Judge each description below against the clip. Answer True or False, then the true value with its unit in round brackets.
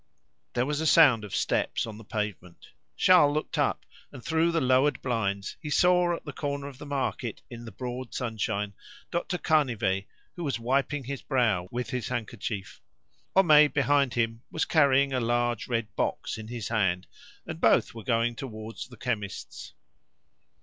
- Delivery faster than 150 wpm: True (170 wpm)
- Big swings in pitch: False (4.3 semitones)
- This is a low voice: True (125 Hz)